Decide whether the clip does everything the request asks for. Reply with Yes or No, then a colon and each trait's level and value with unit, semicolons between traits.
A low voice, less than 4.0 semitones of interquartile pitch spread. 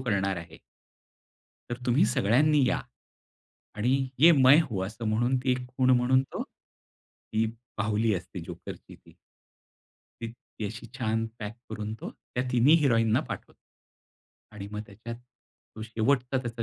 Yes: low, 115 Hz; average, 2.9 semitones